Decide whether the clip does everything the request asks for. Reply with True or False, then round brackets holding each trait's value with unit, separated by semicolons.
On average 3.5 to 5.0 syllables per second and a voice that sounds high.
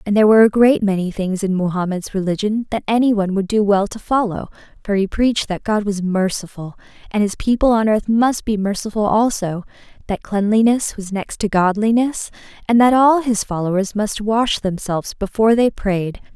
False (5.4 syllables/s; 210 Hz)